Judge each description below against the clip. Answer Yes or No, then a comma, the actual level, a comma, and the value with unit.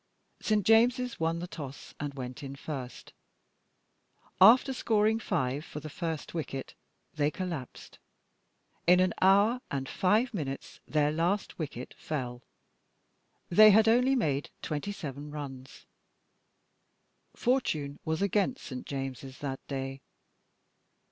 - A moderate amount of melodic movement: No, wide, 7.2 semitones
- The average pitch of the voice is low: No, medium, 155 Hz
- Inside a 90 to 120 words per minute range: Yes, slow, 115 wpm